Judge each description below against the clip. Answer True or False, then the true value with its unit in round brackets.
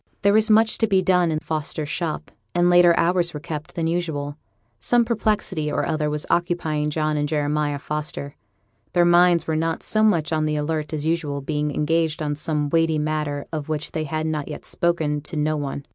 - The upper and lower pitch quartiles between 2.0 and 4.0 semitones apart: True (2.5 semitones)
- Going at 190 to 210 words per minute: True (200 wpm)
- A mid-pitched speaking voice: True (155 Hz)